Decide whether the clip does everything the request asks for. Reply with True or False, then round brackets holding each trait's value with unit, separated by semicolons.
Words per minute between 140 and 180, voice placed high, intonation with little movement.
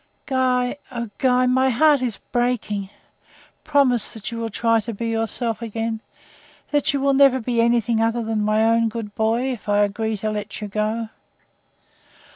True (170 wpm; 230 Hz; 2.3 semitones)